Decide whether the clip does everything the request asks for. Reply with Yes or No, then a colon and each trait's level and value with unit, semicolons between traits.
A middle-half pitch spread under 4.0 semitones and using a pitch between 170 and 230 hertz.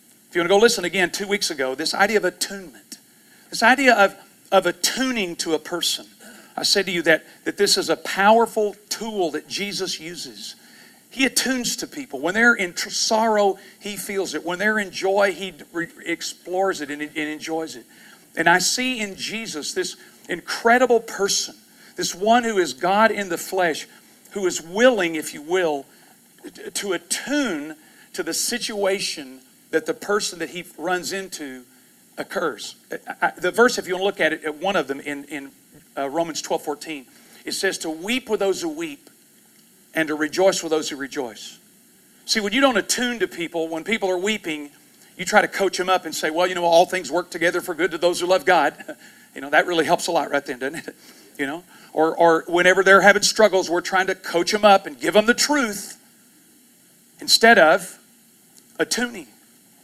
No: average, 5.0 semitones; high, 190 Hz